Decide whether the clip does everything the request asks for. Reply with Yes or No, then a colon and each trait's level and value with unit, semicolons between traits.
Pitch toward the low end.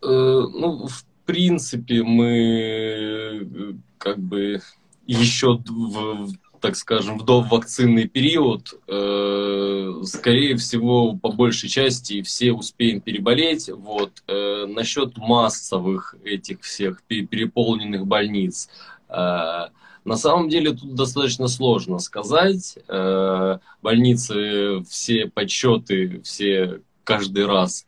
Yes: low, 115 Hz